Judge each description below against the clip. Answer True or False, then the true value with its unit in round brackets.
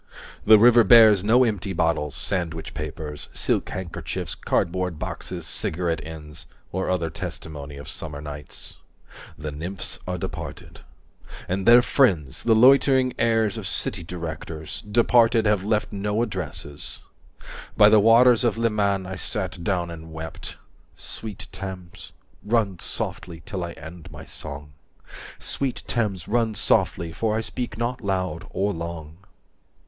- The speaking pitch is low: True (95 Hz)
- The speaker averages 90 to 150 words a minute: True (140 wpm)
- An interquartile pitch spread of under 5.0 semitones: False (5.4 semitones)